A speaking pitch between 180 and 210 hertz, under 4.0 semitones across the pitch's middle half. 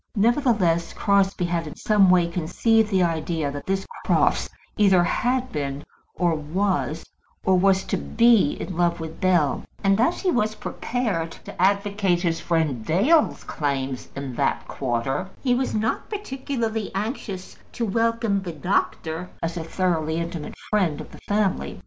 No: medium, 185 Hz; average, 4.7 semitones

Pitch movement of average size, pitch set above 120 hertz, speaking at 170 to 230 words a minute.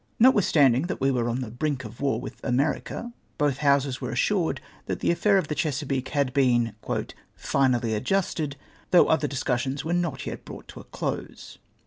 Yes: average, 3.9 semitones; medium, 140 Hz; average, 180 wpm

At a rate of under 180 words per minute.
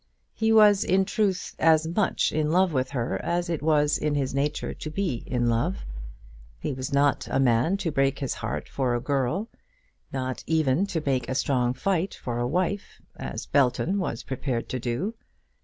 No: average, 185 wpm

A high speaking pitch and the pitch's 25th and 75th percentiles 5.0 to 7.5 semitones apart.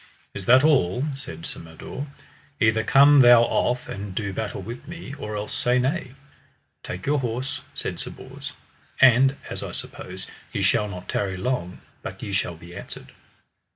No: low, 115 Hz; wide, 5.5 semitones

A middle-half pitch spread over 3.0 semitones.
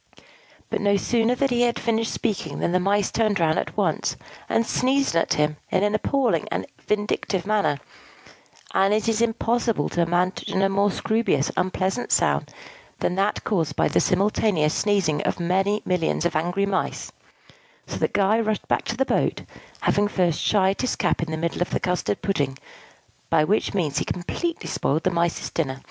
Yes: average, 4.1 semitones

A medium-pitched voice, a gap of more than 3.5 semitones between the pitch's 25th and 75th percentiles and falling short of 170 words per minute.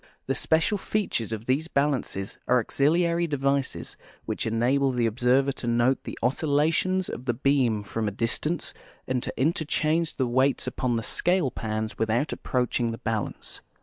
No: low, 130 Hz; average, 4.6 semitones; average, 160 wpm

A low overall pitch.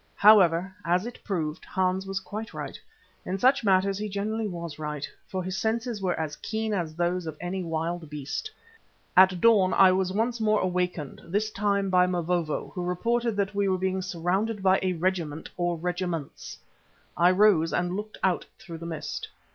No: medium, 185 Hz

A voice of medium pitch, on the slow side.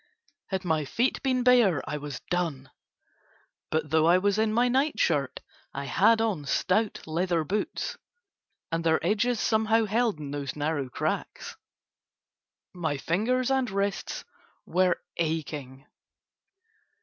Yes: medium, 180 Hz; slow, 130 wpm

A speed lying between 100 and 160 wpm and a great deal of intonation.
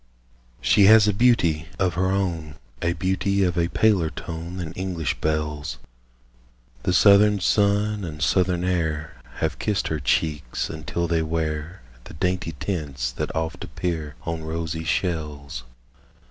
No: average, 140 wpm; average, 3.3 semitones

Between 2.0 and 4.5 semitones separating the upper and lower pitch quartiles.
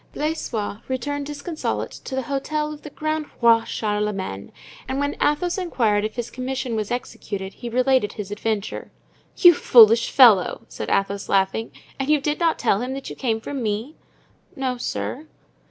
No: average, 5.2 semitones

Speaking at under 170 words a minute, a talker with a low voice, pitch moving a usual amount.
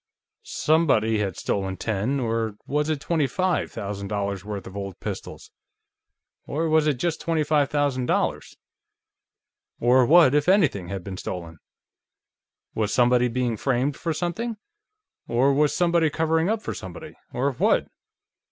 No: average, 145 wpm; low, 130 Hz; wide, 7.1 semitones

